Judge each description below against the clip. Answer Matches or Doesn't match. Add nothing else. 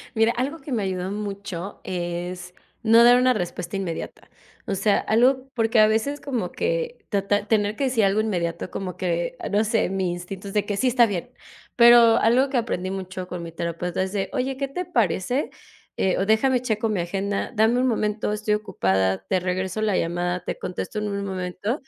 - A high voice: Matches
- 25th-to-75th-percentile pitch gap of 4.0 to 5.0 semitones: Matches